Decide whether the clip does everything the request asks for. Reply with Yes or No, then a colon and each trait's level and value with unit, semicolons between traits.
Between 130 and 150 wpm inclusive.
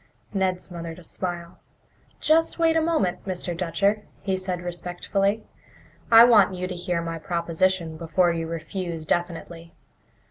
Yes: average, 140 wpm